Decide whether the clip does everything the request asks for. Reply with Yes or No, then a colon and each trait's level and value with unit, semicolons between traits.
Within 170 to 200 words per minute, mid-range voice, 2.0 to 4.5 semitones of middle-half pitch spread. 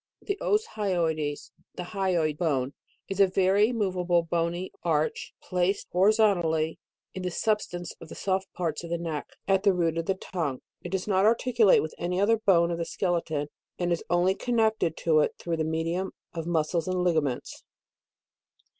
Yes: average, 175 wpm; medium, 175 Hz; average, 2.8 semitones